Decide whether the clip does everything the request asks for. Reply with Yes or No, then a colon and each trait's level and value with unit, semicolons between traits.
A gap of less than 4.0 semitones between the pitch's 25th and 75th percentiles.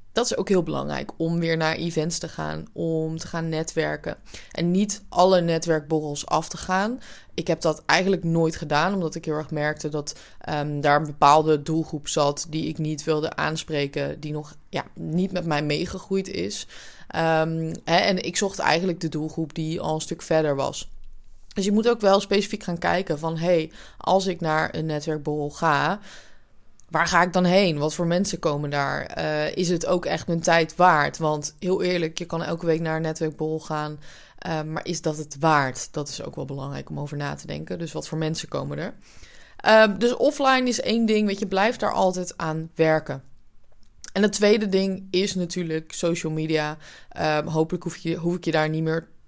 Yes: average, 2.8 semitones